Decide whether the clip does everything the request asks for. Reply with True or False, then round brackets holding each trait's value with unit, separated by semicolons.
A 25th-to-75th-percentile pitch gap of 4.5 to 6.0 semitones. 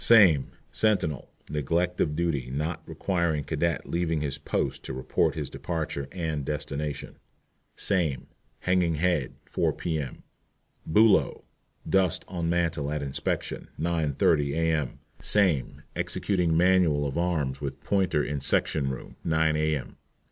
False (3.1 semitones)